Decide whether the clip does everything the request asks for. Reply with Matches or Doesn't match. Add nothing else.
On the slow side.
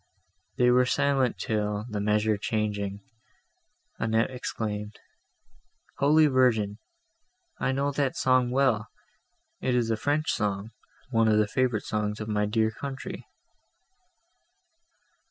Matches